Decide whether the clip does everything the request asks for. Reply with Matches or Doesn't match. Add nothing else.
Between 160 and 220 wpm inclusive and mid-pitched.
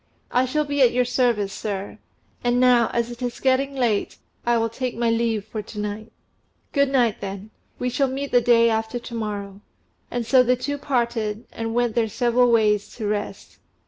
Doesn't match